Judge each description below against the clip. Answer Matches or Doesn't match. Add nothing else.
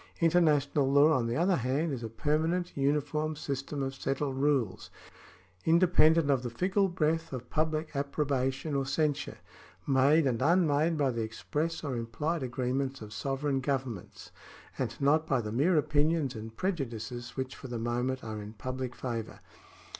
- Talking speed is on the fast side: Doesn't match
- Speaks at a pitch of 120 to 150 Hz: Matches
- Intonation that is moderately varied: Matches